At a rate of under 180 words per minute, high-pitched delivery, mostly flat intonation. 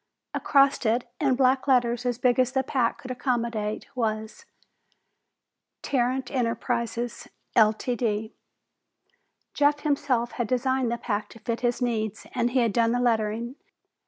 Yes: slow, 135 wpm; high, 240 Hz; narrow, 2.0 semitones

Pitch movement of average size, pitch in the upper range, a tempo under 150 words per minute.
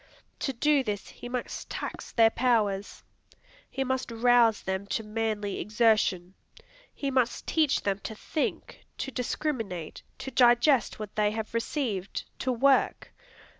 Yes: average, 3.7 semitones; high, 230 Hz; slow, 135 wpm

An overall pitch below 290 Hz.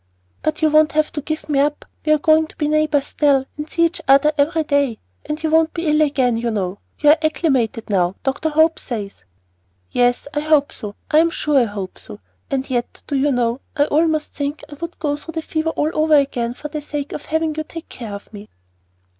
No: very high, 295 Hz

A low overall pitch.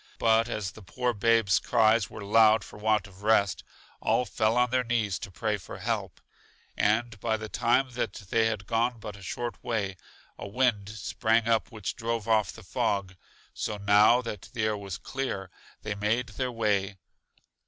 Yes: low, 110 Hz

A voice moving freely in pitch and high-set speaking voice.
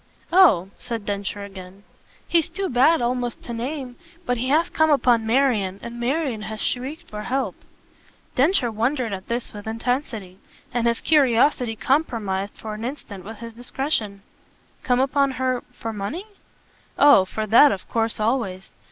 No: average, 4.2 semitones; high, 235 Hz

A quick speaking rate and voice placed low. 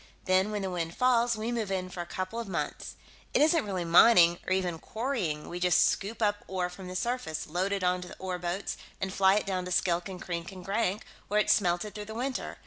No: fast, 230 wpm; high, 190 Hz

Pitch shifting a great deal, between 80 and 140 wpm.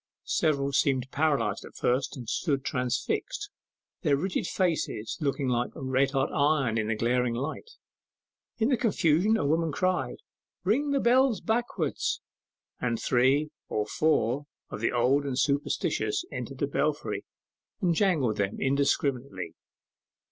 Yes: wide, 6.0 semitones; slow, 135 wpm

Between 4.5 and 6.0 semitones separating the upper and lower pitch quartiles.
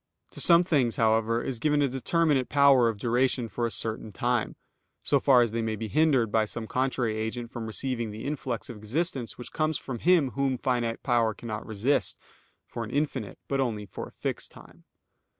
No: average, 3.5 semitones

